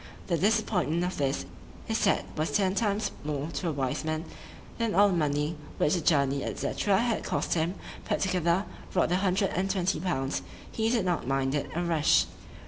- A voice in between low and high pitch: Yes, medium, 175 Hz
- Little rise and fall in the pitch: No, average, 4.5 semitones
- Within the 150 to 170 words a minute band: No, average, 180 wpm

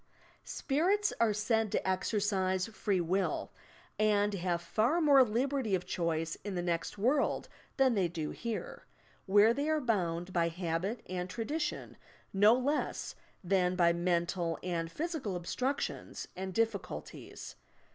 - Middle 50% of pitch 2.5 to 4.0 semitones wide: No, average, 5.0 semitones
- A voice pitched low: No, high, 200 Hz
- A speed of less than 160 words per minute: Yes, average, 140 wpm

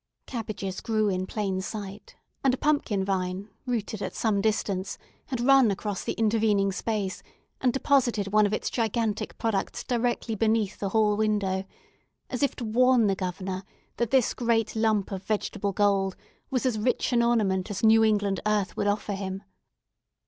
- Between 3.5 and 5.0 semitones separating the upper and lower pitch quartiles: No, average, 2.7 semitones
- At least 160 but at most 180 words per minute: Yes, average, 165 wpm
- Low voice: No, high, 215 Hz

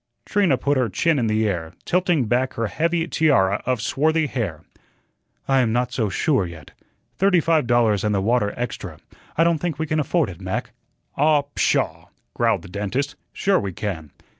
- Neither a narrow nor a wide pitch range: No, wide, 7.1 semitones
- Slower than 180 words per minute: No, average, 185 wpm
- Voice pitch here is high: No, low, 125 Hz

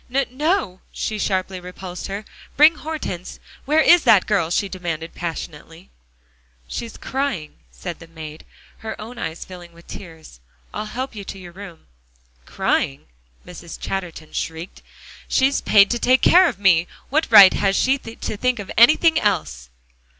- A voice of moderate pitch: No, high, 195 Hz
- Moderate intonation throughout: No, wide, 6.6 semitones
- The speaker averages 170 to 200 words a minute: No, average, 155 wpm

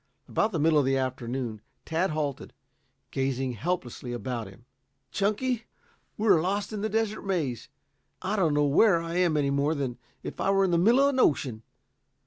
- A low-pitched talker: No, medium, 155 Hz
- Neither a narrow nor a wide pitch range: No, wide, 6.9 semitones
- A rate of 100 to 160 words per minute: No, average, 180 wpm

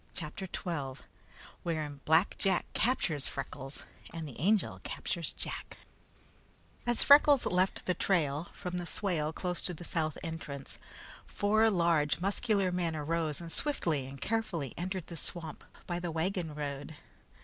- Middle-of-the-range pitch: Yes, medium, 170 Hz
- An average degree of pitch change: Yes, average, 3.7 semitones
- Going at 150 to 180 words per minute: No, average, 140 wpm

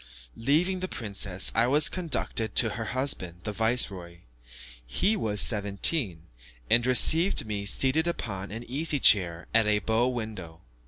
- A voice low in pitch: Yes, low, 110 Hz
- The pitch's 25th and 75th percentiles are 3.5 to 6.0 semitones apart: Yes, average, 5.2 semitones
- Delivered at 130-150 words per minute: Yes, average, 145 wpm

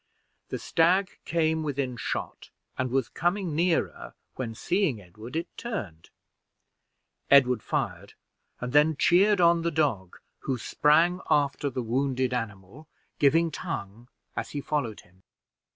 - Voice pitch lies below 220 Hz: Yes, medium, 140 Hz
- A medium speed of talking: No, slow, 130 wpm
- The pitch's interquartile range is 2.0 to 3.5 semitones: No, wide, 5.5 semitones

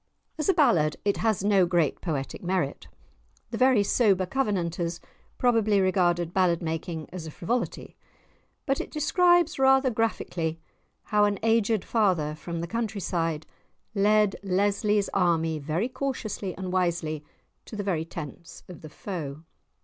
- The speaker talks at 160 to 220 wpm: No, average, 140 wpm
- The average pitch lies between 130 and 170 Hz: No, high, 190 Hz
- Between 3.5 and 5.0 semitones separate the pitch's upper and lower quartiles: Yes, average, 4.6 semitones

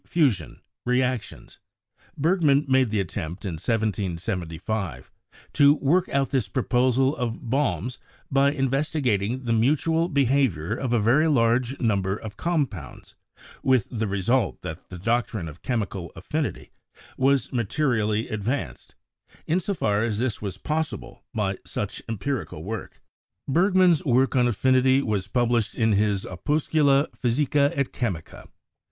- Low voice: Yes, low, 120 Hz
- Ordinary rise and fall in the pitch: Yes, average, 5.0 semitones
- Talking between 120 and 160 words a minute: Yes, slow, 135 wpm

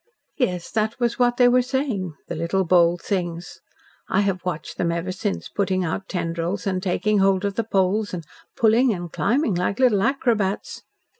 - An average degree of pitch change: Yes, average, 4.0 semitones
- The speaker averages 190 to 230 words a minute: No, average, 175 wpm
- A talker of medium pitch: No, high, 195 Hz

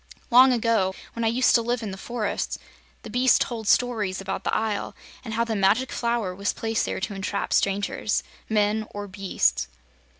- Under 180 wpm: No, average, 185 wpm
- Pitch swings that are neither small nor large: Yes, average, 3.0 semitones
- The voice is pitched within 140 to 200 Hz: No, high, 220 Hz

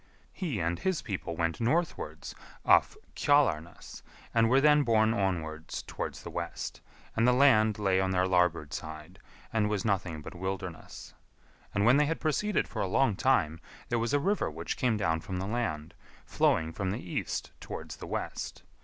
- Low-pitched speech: Yes, low, 100 Hz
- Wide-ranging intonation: Yes, wide, 6.5 semitones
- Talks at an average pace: Yes, average, 175 wpm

